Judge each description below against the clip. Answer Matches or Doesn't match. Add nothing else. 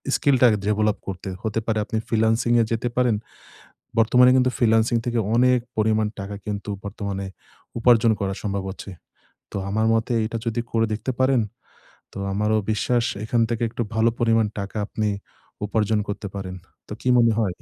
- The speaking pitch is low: Matches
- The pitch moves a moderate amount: Doesn't match